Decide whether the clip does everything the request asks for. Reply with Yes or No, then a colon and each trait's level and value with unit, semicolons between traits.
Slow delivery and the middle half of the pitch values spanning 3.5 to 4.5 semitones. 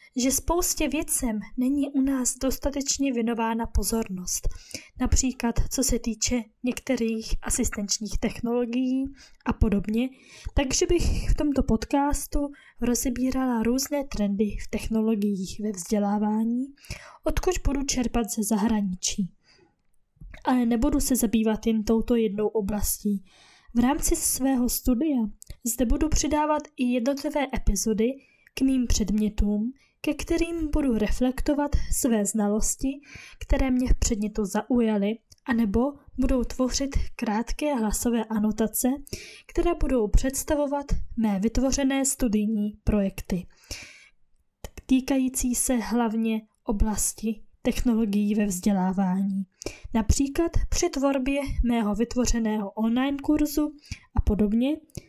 Yes: slow, 105 wpm; average, 3.9 semitones